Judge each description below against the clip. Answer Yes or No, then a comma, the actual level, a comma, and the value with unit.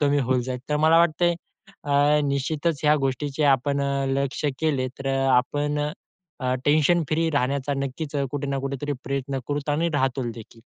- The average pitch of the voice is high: No, medium, 140 Hz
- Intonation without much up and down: Yes, narrow, 1.8 semitones